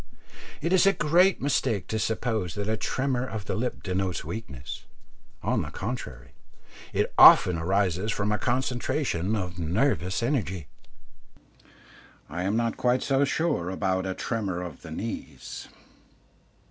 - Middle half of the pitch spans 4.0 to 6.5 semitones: Yes, wide, 5.6 semitones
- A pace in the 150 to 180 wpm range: No, average, 140 wpm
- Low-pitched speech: Yes, low, 105 Hz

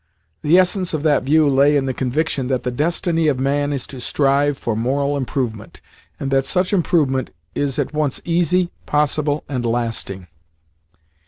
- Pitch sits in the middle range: Yes, medium, 145 Hz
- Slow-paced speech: No, average, 165 wpm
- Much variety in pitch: No, average, 3.0 semitones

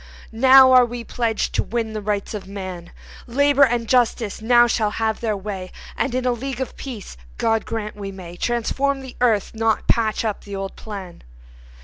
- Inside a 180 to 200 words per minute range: Yes, average, 190 wpm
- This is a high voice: Yes, high, 225 Hz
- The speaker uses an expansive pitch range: No, average, 3.1 semitones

